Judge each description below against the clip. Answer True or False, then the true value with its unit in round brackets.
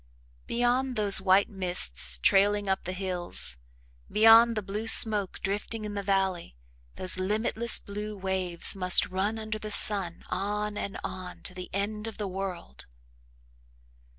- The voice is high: True (200 Hz)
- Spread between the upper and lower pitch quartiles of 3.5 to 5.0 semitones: False (2.4 semitones)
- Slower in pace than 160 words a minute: True (145 wpm)